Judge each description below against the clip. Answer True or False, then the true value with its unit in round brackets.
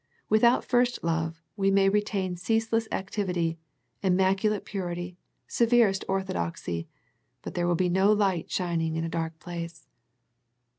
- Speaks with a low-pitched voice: False (185 Hz)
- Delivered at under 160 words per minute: True (135 wpm)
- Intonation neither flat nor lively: True (3.6 semitones)